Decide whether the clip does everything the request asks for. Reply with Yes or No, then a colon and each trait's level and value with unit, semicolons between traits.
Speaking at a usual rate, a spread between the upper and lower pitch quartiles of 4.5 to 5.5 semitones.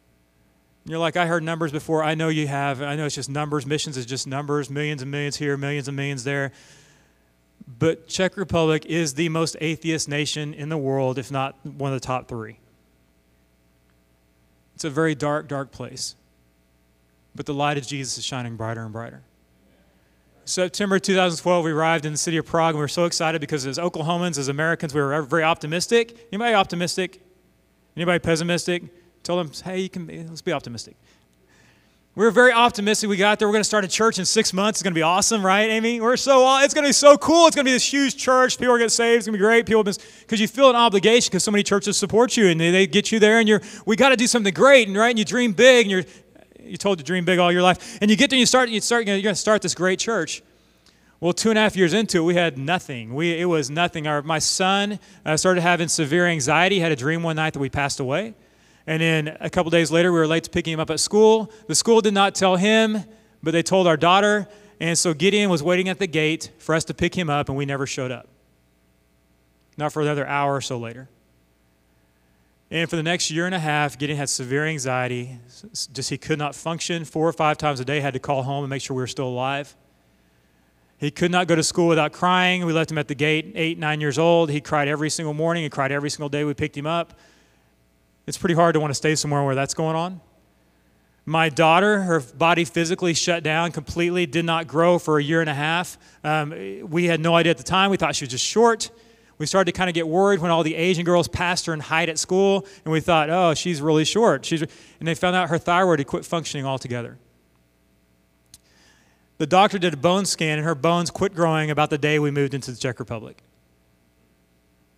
No: fast, 235 wpm; average, 4.8 semitones